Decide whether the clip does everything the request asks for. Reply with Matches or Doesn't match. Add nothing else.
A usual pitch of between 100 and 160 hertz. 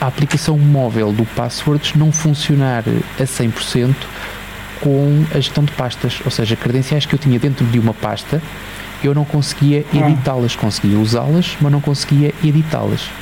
Matches